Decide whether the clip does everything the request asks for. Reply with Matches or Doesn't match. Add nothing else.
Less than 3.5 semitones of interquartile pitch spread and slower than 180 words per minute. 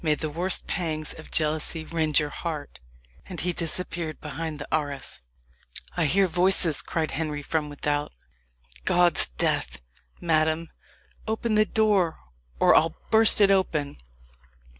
Matches